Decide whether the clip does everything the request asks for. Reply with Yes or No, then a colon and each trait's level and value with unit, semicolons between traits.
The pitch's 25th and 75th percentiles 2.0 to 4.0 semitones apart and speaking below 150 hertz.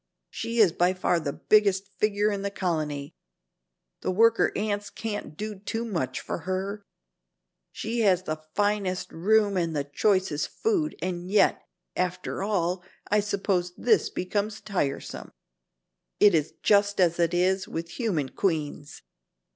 No: average, 3.4 semitones; high, 190 Hz